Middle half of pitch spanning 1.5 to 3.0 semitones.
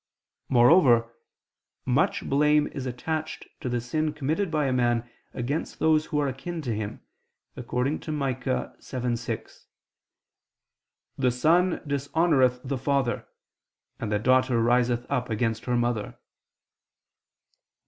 No: average, 3.7 semitones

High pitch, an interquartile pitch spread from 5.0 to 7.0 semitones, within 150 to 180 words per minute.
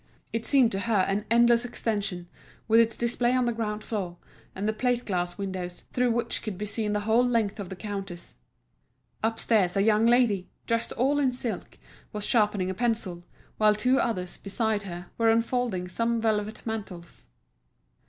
No: high, 215 Hz; average, 3.0 semitones; average, 175 wpm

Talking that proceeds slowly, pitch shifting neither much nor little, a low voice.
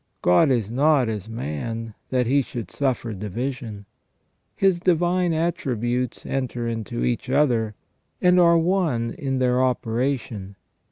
Yes: slow, 125 wpm; average, 4.7 semitones; low, 125 Hz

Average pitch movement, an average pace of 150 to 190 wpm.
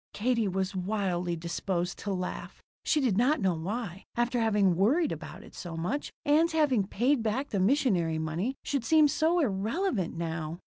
No: wide, 6.9 semitones; average, 170 wpm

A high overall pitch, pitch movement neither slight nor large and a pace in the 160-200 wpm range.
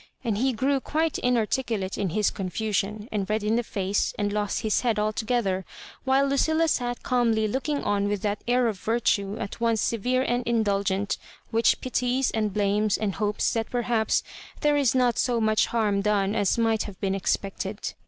Yes: high, 220 Hz; average, 3.0 semitones; average, 185 wpm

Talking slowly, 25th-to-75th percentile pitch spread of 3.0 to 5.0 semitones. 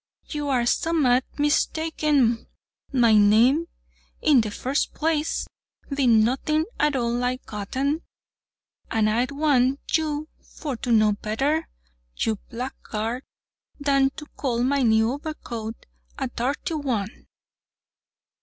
Yes: slow, 115 wpm; average, 4.3 semitones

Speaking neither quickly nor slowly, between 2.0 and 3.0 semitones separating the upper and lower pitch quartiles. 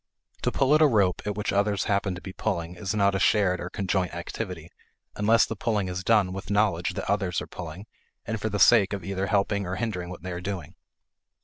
No: fast, 225 wpm; narrow, 2.4 semitones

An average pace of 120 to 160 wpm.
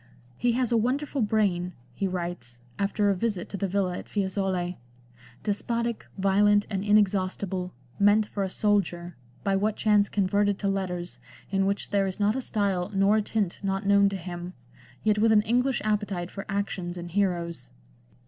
No: average, 185 wpm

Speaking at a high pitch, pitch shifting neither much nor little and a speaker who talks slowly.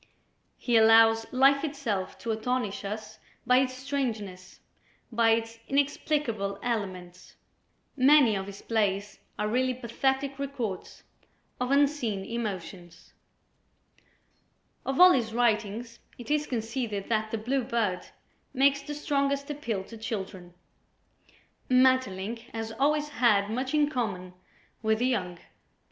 Yes: high, 230 Hz; average, 4.2 semitones; slow, 120 wpm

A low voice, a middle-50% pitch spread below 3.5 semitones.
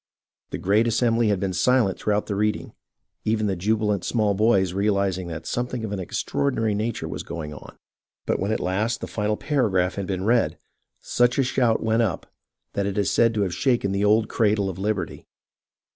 Yes: low, 105 Hz; average, 2.8 semitones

